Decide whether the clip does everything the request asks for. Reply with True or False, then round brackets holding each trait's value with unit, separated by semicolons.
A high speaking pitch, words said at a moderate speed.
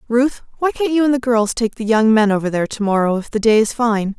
False (230 Hz; 285 wpm)